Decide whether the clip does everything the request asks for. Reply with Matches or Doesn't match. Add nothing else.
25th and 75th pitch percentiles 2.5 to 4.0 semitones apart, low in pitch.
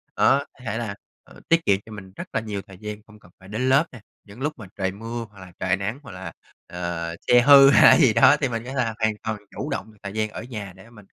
Matches